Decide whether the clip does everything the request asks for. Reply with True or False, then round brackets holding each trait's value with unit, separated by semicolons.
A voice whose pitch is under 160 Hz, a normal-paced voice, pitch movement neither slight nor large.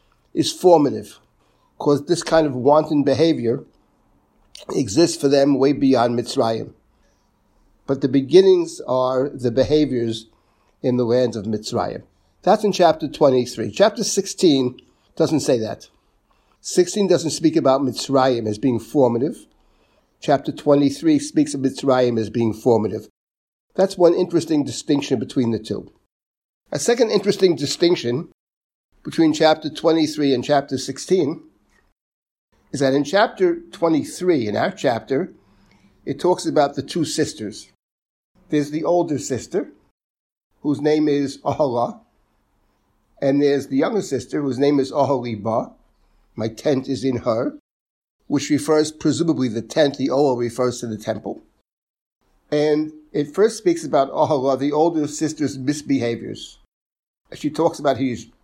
False (140 Hz; 130 wpm; 4.2 semitones)